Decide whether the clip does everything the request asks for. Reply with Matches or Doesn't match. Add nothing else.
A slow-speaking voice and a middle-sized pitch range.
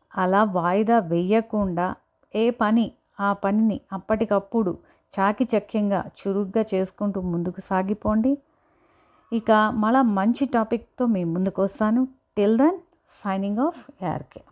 Doesn't match